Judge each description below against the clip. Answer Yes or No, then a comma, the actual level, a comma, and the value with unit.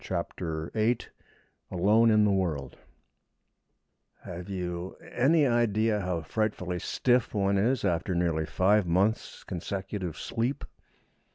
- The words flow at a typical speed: No, slow, 110 wpm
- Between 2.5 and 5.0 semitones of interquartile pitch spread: Yes, average, 4.0 semitones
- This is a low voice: Yes, very low, 95 Hz